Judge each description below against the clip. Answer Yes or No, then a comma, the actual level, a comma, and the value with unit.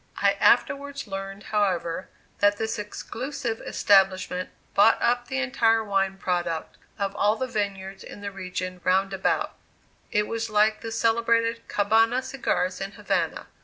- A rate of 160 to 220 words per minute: No, average, 140 wpm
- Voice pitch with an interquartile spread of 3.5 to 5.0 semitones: No, average, 2.9 semitones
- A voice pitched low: No, high, 205 Hz